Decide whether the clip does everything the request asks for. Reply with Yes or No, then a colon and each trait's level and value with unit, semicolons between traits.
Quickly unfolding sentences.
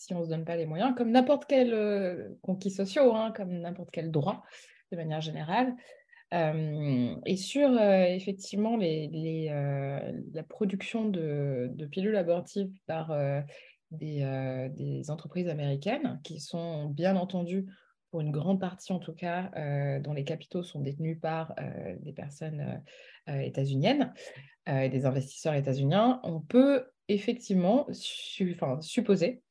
No: average, 155 wpm